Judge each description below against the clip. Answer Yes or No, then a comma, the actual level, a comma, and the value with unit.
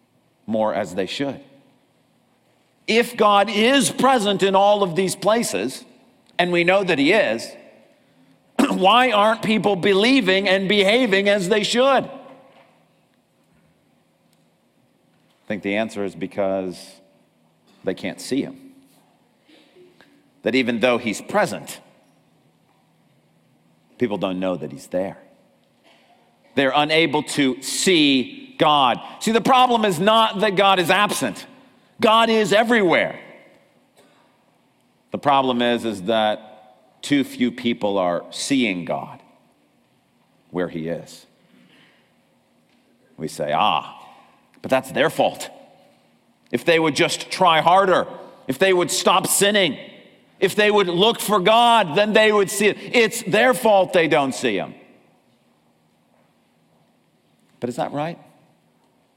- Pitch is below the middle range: No, high, 195 Hz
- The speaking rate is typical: No, slow, 120 wpm